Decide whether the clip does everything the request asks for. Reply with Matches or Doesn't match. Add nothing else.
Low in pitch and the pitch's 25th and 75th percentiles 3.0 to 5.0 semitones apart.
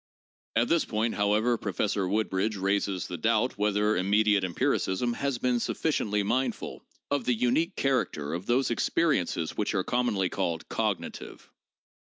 Matches